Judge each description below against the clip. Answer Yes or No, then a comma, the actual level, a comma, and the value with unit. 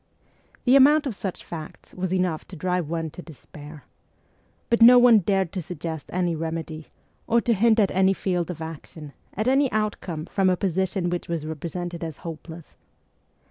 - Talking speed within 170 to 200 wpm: Yes, average, 175 wpm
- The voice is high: No, medium, 180 Hz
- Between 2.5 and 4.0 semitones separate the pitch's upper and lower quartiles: Yes, average, 3.6 semitones